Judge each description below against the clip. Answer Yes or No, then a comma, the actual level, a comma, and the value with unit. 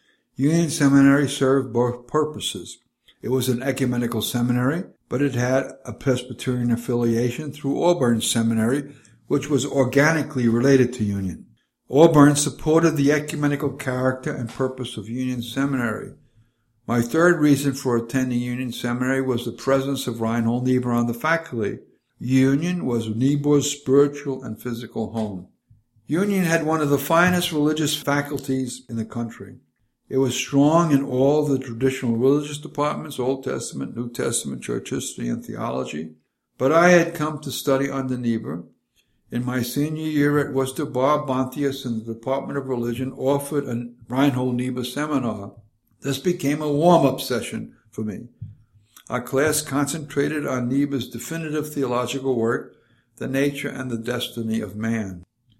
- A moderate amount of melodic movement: Yes, average, 3.2 semitones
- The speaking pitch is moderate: No, low, 130 Hz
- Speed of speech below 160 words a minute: Yes, average, 145 wpm